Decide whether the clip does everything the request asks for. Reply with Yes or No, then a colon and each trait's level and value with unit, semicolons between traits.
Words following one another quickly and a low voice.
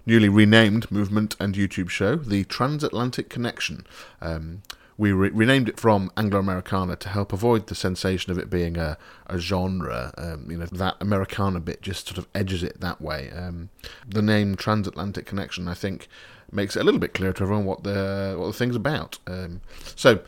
No: average, 190 wpm; very low, 95 Hz